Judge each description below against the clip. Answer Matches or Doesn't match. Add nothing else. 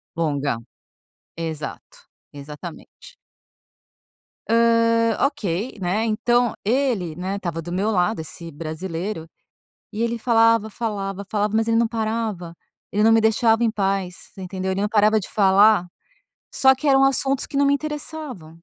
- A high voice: Matches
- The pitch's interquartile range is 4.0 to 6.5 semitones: Matches